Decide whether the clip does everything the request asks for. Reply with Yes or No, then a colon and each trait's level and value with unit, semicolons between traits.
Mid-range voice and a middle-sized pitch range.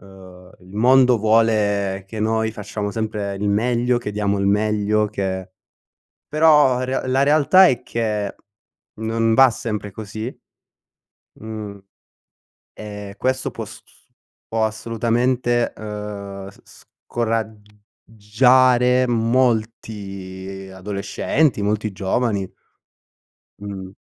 No: low, 110 Hz; average, 3.0 semitones